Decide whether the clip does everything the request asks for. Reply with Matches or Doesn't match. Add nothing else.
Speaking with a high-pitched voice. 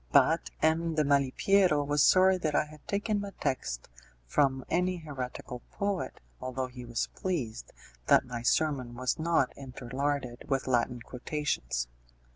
Doesn't match